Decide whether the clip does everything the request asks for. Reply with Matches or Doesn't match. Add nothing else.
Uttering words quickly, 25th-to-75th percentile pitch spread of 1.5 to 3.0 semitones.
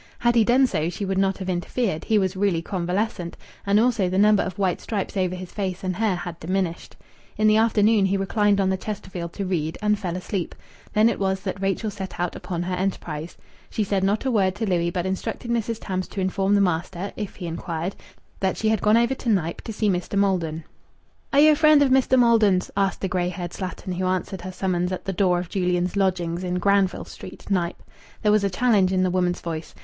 Matches